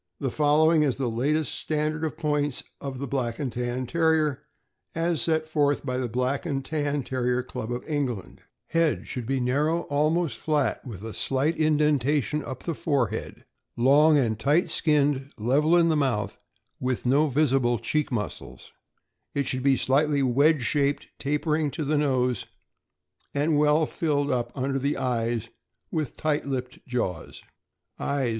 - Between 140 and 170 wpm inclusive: Yes, average, 155 wpm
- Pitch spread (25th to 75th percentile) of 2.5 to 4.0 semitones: Yes, average, 3.2 semitones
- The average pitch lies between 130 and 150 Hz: Yes, medium, 140 Hz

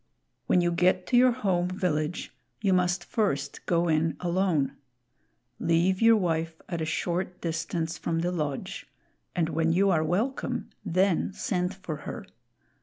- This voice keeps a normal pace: Yes, average, 150 wpm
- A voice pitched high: No, medium, 175 Hz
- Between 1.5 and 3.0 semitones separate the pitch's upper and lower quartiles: Yes, narrow, 2.4 semitones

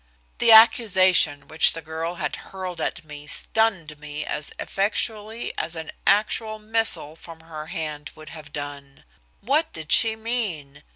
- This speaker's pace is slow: No, average, 150 wpm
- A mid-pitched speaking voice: Yes, medium, 165 Hz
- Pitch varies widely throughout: Yes, wide, 6.1 semitones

